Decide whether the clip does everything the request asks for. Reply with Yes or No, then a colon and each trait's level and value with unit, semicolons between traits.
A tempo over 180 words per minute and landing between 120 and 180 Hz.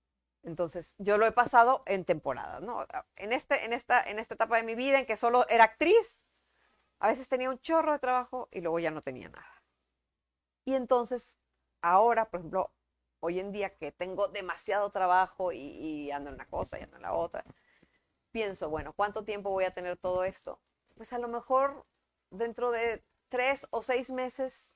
No: fast, 190 wpm; high, 215 Hz